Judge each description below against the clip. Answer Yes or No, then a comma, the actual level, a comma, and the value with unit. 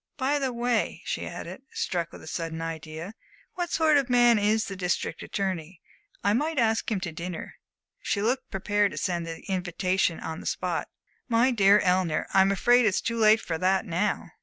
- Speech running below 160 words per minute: No, average, 190 wpm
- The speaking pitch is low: No, high, 195 Hz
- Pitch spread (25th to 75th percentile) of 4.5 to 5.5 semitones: Yes, average, 5.1 semitones